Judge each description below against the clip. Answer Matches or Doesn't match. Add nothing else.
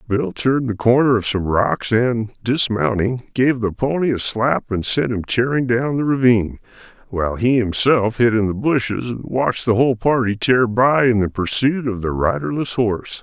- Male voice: Matches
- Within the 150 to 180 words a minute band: Doesn't match